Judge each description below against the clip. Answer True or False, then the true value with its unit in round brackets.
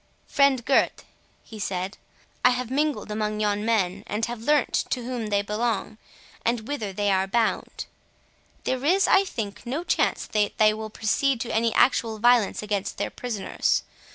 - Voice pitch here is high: True (225 Hz)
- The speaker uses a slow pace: False (165 wpm)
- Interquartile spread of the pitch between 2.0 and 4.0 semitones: True (3.0 semitones)